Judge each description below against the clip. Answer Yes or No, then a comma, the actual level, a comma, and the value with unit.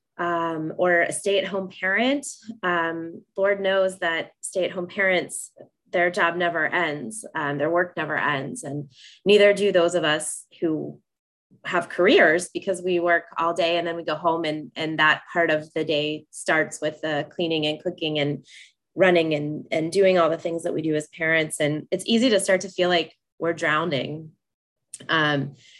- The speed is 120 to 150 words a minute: No, average, 175 wpm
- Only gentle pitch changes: No, average, 3.1 semitones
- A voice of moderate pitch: Yes, medium, 170 Hz